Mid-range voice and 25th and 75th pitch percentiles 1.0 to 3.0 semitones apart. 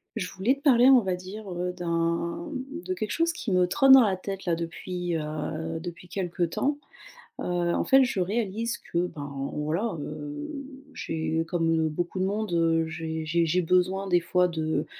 No: medium, 180 Hz; average, 3.8 semitones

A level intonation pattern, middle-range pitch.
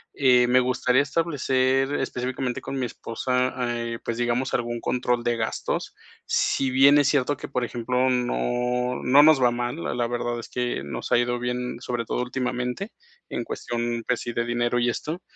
No: narrow, 1.5 semitones; low, 125 Hz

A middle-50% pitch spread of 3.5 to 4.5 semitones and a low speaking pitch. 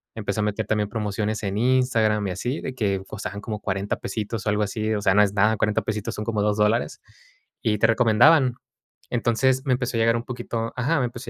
No: narrow, 2.4 semitones; low, 110 Hz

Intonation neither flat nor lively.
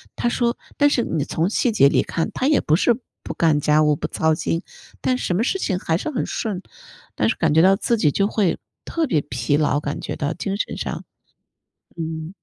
No: wide, 6.8 semitones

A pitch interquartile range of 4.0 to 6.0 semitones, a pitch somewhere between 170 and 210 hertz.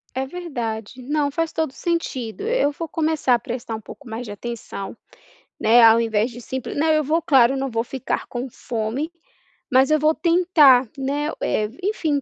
No: average, 4.8 semitones; very high, 265 Hz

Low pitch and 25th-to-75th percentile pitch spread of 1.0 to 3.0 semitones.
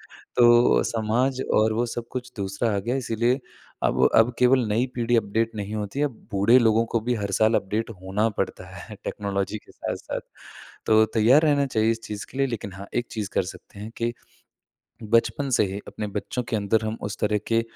Yes: low, 115 Hz; narrow, 2.5 semitones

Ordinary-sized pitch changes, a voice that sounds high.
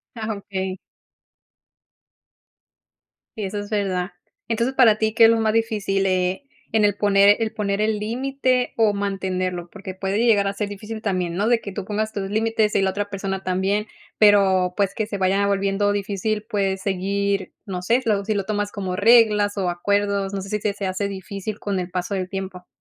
No: narrow, 1.9 semitones; high, 200 Hz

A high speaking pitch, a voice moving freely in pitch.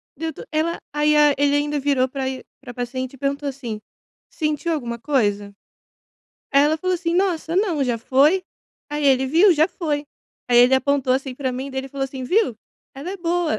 No: very high, 280 Hz; average, 3.2 semitones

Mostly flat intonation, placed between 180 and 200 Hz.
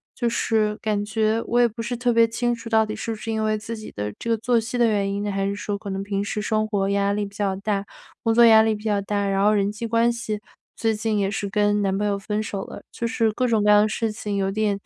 No: narrow, 2.0 semitones; high, 215 Hz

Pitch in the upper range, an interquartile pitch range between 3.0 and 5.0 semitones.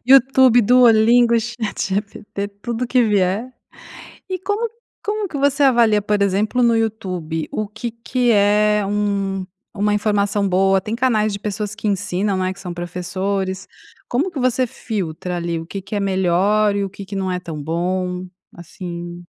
Yes: high, 205 Hz; average, 3.7 semitones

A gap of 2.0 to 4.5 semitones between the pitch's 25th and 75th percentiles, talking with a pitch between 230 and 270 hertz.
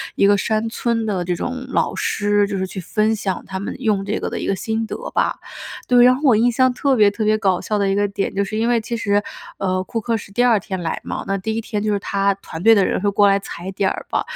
No: narrow, 2.5 semitones; high, 205 Hz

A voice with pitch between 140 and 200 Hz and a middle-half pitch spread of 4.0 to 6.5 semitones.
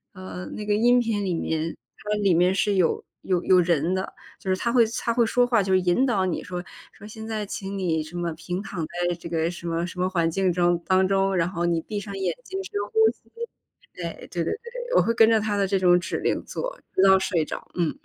No: medium, 185 Hz; average, 3.1 semitones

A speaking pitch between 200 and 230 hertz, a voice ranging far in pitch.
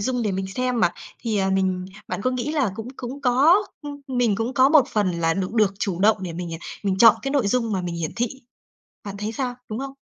No: high, 220 Hz; average, 4.9 semitones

